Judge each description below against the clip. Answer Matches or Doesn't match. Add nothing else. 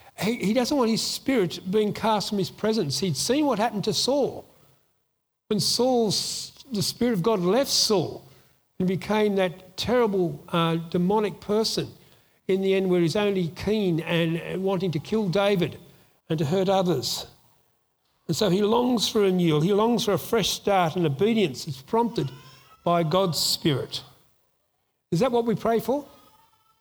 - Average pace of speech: Matches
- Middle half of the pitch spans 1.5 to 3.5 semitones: Doesn't match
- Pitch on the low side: Doesn't match